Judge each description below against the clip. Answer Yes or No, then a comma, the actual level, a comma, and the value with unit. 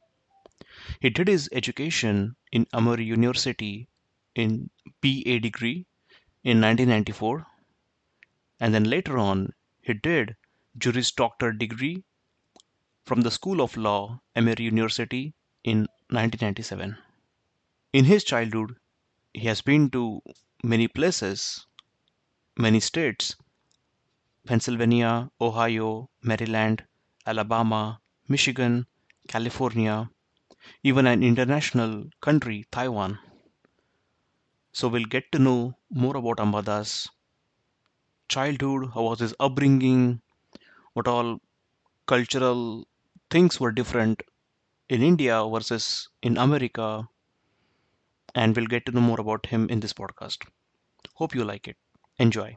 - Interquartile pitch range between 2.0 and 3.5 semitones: Yes, narrow, 2.6 semitones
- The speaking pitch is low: Yes, low, 120 Hz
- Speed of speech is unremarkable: Yes, average, 105 wpm